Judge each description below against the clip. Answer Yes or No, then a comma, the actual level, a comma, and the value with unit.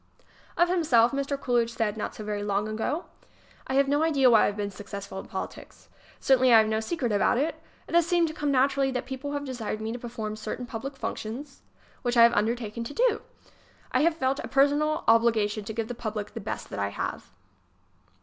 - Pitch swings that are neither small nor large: Yes, average, 4.4 semitones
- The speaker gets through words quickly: Yes, fast, 215 wpm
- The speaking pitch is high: Yes, high, 240 Hz